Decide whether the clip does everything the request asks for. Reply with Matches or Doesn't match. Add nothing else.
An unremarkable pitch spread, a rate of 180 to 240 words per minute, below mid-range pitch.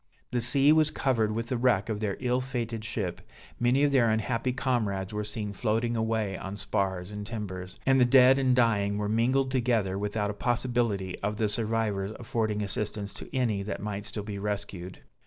Matches